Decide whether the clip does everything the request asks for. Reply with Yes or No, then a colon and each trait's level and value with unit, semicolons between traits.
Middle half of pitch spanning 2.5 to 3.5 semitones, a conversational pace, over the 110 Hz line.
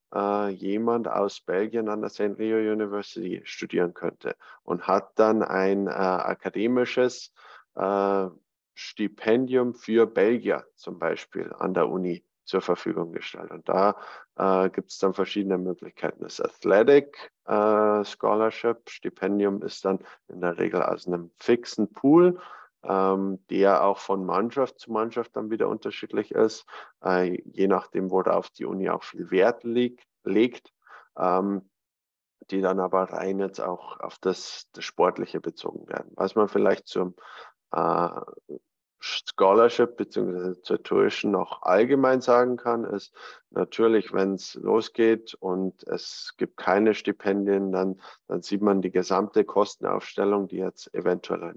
No: average, 3.0 semitones; average, 140 wpm; low, 100 Hz